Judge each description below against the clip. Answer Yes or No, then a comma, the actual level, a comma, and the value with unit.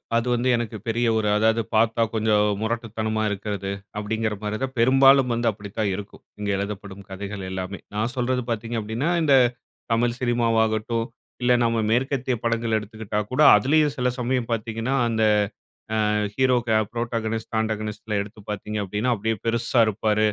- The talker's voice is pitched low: Yes, low, 115 Hz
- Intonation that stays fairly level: Yes, narrow, 2.1 semitones